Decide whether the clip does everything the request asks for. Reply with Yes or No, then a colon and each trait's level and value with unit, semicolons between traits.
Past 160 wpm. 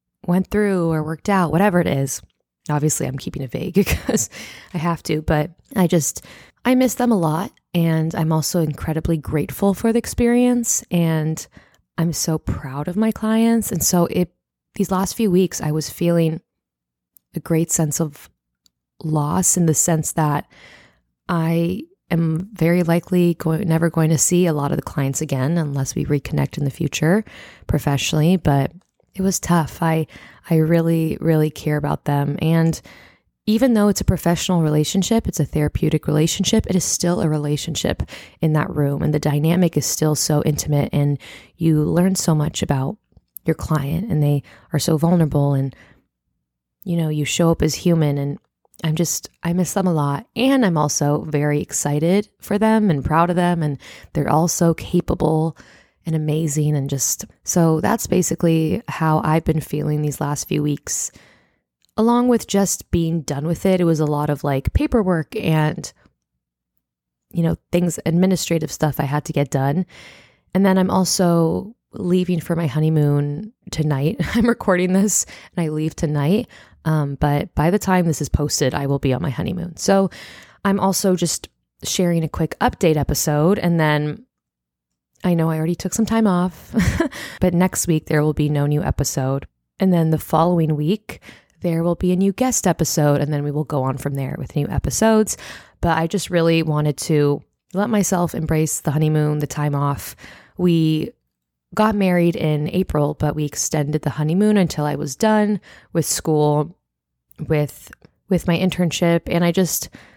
Yes: average, 175 wpm